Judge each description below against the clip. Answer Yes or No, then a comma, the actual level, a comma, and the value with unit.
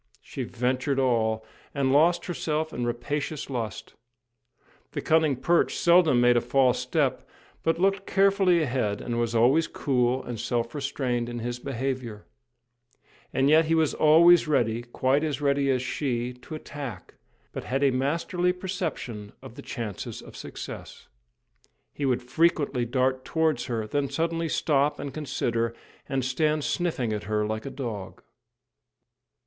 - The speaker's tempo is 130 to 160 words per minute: Yes, average, 150 wpm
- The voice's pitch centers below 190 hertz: Yes, low, 135 Hz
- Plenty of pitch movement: No, average, 4.4 semitones